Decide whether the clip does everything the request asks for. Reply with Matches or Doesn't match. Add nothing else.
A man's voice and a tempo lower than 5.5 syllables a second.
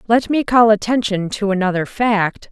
Doesn't match